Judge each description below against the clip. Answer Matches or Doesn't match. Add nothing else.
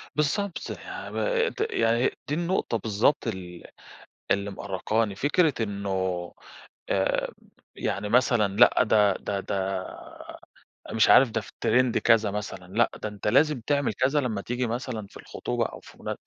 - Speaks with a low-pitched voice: Matches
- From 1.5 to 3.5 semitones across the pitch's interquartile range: Doesn't match